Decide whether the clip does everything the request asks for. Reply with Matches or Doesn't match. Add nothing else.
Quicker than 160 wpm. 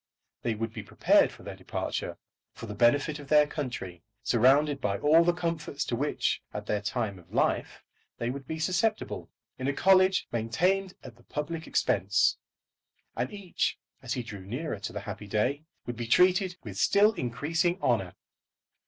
Matches